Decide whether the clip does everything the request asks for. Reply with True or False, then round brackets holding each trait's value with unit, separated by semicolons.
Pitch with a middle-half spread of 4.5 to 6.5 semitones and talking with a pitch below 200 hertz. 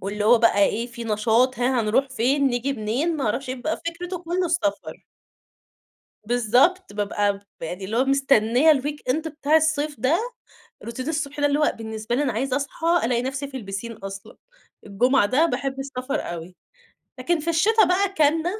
False (5.0 semitones; 265 Hz)